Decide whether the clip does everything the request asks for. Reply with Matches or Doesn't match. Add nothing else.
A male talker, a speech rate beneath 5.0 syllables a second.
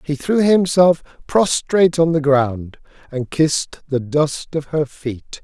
Matches